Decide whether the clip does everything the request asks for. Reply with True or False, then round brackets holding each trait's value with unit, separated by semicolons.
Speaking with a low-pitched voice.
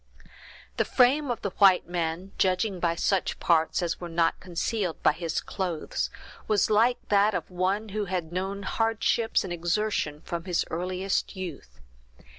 False (185 Hz)